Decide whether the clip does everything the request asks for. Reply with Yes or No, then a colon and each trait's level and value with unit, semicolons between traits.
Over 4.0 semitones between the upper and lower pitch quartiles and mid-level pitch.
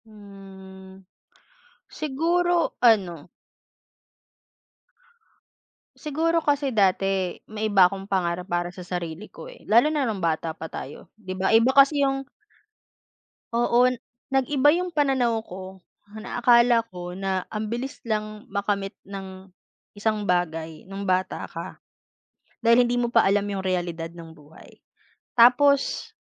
No: average, 4.7 semitones; high, 205 Hz